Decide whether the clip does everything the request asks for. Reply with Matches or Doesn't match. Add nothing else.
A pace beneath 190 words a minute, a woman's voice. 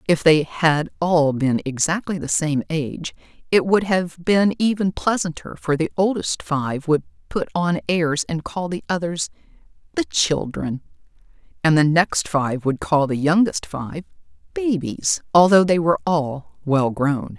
Matches